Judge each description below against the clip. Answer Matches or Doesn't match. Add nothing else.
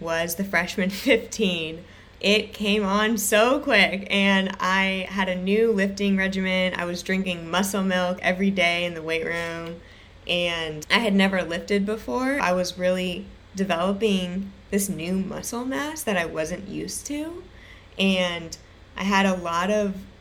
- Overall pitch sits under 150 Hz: Doesn't match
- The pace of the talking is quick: Doesn't match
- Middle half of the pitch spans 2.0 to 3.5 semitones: Matches